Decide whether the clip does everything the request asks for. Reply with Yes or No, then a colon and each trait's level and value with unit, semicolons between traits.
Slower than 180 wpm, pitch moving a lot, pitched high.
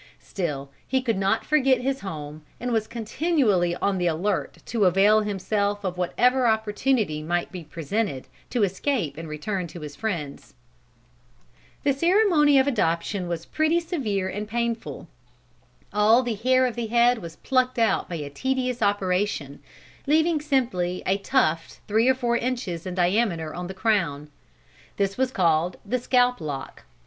Yes: average, 155 wpm; wide, 6.3 semitones; high, 210 Hz